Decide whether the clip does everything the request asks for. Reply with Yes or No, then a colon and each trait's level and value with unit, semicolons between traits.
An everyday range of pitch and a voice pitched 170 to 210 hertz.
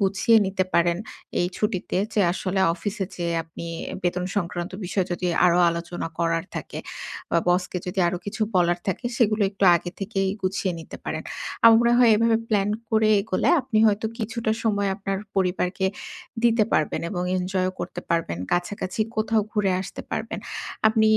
Yes: average, 3.4 semitones; high, 190 Hz